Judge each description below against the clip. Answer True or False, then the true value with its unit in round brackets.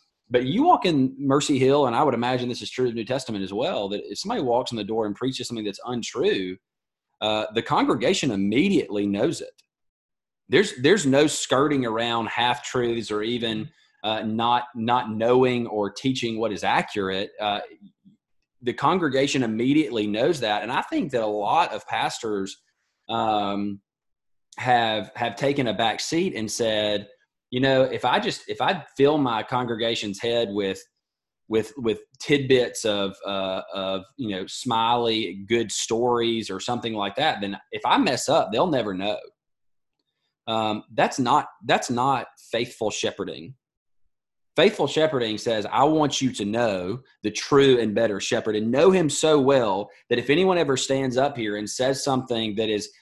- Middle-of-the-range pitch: False (115 Hz)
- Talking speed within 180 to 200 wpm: False (170 wpm)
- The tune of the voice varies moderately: True (3.9 semitones)